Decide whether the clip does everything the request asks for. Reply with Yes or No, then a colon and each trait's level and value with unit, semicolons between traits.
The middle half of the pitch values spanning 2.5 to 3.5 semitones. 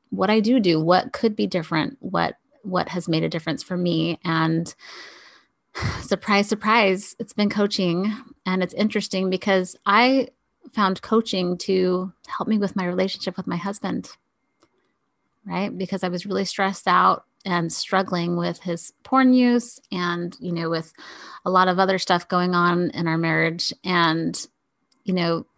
Yes: average, 3.0 semitones